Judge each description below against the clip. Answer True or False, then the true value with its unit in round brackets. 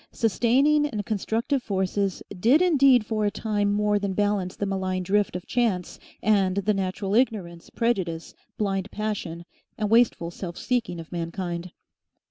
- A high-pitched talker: True (205 Hz)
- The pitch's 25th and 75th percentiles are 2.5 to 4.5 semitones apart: True (3.4 semitones)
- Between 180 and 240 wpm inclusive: False (145 wpm)